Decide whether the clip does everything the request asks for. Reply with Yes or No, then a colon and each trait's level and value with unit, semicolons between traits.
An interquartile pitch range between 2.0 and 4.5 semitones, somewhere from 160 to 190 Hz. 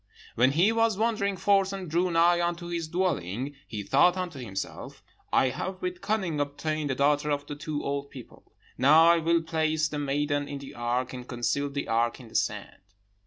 No: average, 4.0 semitones; medium, 150 Hz